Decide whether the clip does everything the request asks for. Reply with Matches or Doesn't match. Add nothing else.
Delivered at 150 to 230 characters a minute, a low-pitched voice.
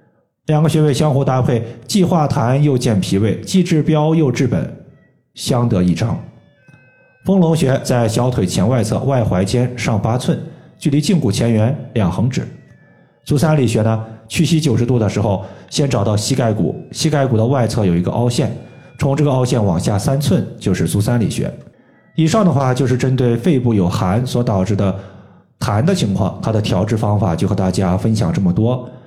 Doesn't match